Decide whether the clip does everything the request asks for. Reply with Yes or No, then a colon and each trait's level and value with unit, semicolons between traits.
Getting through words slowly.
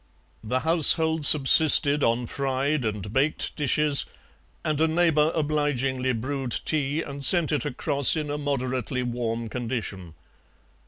Yes: slow, 125 wpm